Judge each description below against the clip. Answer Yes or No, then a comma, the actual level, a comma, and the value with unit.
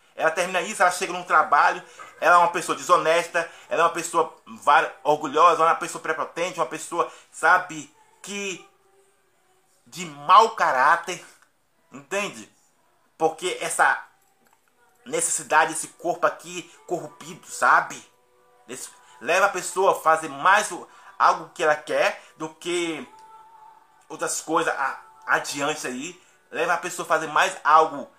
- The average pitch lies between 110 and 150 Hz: No, medium, 175 Hz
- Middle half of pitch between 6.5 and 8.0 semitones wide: No, average, 5.1 semitones